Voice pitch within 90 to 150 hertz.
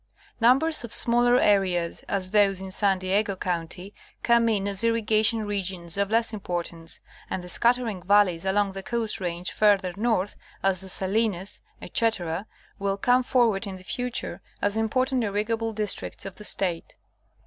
No: high, 200 Hz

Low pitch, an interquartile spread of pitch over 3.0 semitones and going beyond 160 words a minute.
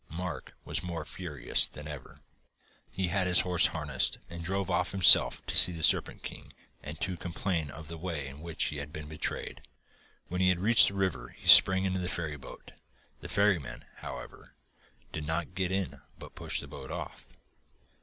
Yes: very low, 85 Hz; average, 3.4 semitones; average, 180 wpm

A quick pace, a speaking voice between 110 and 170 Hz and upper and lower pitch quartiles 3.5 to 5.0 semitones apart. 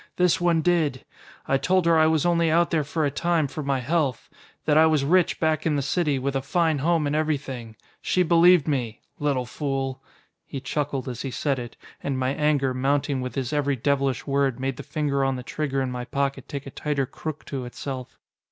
No: fast, 215 wpm; medium, 140 Hz; average, 2.9 semitones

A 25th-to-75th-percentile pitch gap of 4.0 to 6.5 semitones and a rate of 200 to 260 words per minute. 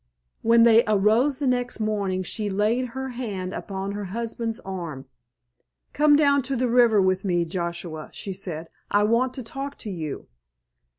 No: average, 4.8 semitones; average, 165 wpm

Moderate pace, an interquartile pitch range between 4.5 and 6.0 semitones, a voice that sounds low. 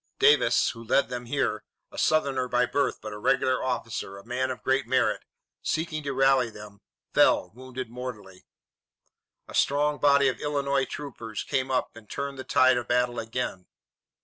No: average, 170 wpm; average, 2.9 semitones; low, 130 Hz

